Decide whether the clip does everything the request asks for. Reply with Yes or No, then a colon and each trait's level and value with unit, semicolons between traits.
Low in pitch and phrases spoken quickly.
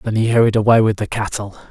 Yes: low, 110 Hz; fast, 245 wpm